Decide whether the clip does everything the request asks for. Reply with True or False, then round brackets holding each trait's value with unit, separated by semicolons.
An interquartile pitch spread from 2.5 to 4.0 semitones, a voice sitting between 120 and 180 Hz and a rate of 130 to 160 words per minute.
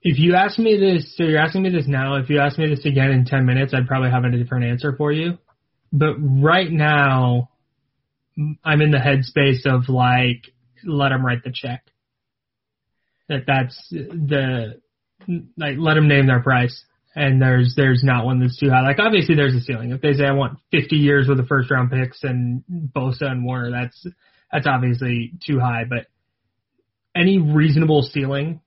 False (3.2 semitones; 140 Hz; 185 wpm)